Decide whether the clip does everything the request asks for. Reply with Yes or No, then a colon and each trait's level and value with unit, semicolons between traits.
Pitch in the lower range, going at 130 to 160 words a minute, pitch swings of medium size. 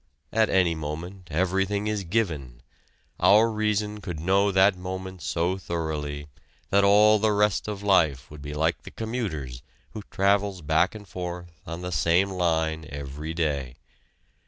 Yes: very low, 90 Hz; average, 150 wpm; average, 4.2 semitones